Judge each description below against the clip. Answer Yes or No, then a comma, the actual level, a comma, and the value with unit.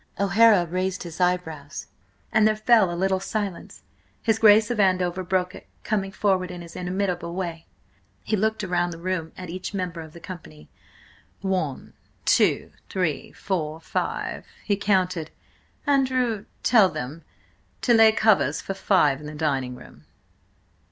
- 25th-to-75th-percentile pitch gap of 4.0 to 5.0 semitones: No, average, 3.4 semitones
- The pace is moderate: Yes, average, 145 wpm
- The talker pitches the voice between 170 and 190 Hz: Yes, medium, 185 Hz